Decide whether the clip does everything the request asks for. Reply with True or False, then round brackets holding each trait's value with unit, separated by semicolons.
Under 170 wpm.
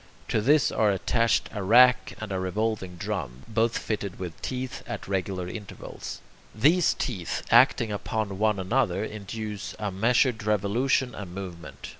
True (145 wpm)